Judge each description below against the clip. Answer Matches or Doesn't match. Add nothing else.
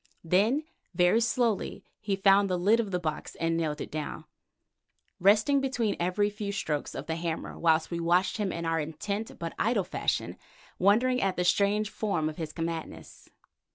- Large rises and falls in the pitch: Doesn't match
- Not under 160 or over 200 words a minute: Matches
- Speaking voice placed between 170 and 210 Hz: Matches